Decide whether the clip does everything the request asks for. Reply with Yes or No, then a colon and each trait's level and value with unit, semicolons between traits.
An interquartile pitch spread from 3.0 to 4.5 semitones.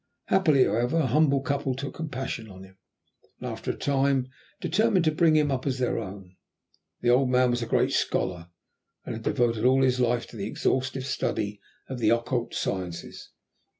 Yes: average, 3.4 semitones